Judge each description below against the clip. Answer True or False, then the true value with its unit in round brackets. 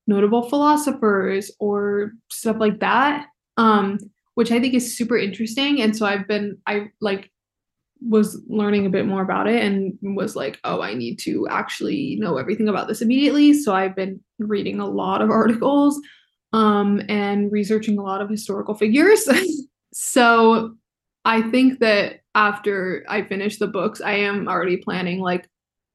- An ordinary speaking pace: True (160 wpm)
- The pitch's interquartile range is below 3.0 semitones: True (2.4 semitones)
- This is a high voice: True (210 Hz)